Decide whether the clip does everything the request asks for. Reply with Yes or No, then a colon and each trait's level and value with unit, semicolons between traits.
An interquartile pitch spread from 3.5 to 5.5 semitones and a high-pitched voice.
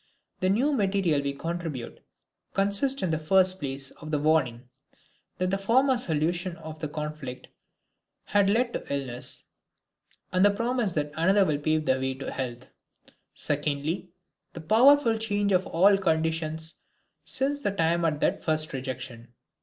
No: average, 5.2 semitones; medium, 165 Hz